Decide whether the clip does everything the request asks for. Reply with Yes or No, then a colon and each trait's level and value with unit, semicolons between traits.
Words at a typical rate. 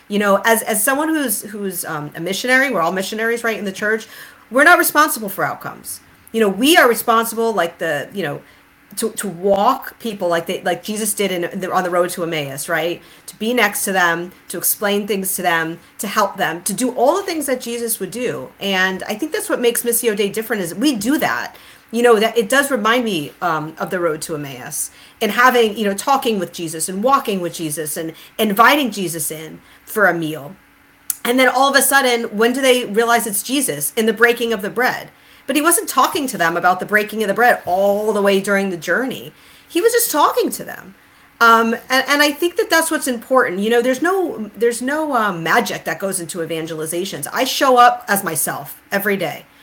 No: fast, 220 wpm